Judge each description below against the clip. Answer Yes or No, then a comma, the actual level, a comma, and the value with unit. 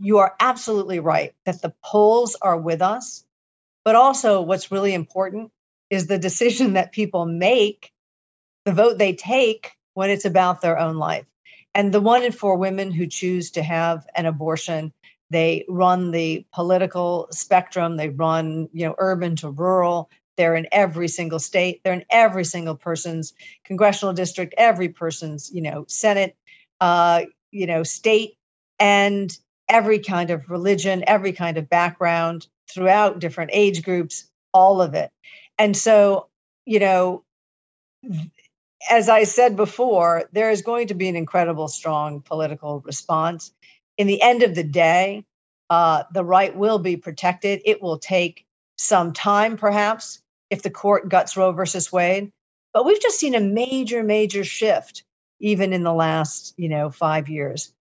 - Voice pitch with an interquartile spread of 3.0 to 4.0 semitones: Yes, average, 3.6 semitones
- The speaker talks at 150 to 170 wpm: Yes, average, 155 wpm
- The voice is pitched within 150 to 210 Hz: Yes, medium, 185 Hz